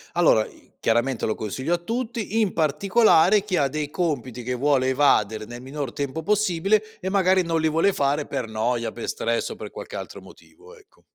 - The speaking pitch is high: No, medium, 150 Hz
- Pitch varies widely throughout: Yes, wide, 7.1 semitones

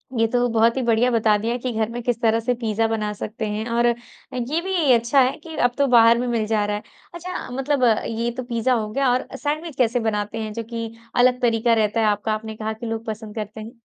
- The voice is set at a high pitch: Yes, high, 230 Hz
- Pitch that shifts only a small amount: Yes, narrow, 2.2 semitones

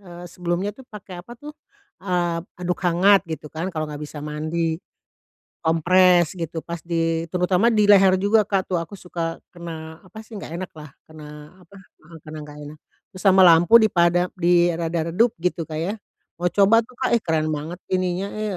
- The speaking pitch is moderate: Yes, medium, 175 Hz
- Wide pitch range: No, average, 2.8 semitones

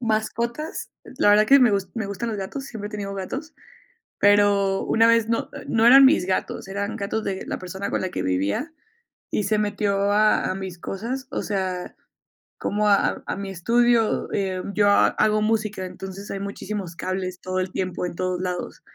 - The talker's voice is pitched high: Yes, high, 200 Hz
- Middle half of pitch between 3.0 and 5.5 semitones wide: No, narrow, 2.6 semitones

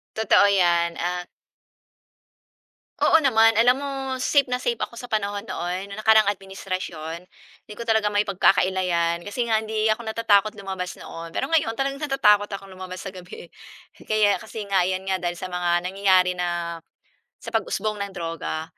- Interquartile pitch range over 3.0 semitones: Yes, average, 3.6 semitones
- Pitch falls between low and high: No, high, 195 Hz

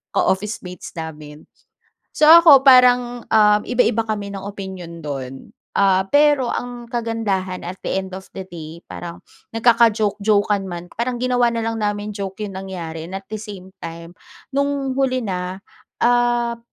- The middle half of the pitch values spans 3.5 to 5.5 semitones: Yes, average, 4.4 semitones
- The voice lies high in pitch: Yes, high, 205 Hz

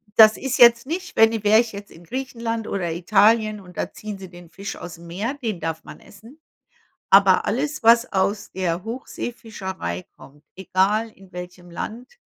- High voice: Yes, high, 205 Hz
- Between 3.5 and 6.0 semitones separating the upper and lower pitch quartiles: Yes, average, 4.3 semitones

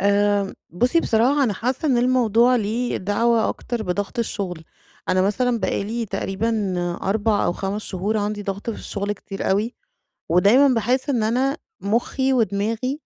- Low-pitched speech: No, high, 220 Hz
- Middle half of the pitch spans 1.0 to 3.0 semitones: No, average, 3.4 semitones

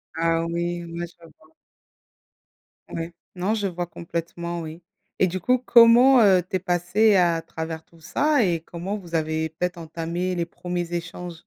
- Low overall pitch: No, medium, 175 Hz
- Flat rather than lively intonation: Yes, narrow, 2.0 semitones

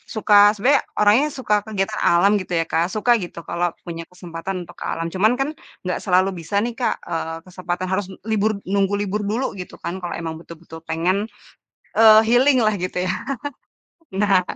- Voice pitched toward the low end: No, high, 190 Hz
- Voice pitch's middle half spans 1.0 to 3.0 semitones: No, average, 3.5 semitones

